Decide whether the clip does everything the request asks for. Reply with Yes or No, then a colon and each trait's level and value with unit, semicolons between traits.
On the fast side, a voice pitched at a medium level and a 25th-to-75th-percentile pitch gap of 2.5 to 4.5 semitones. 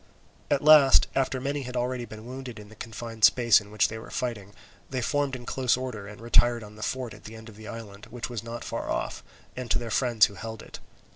No: fast, 240 wpm; low, 115 Hz; average, 2.8 semitones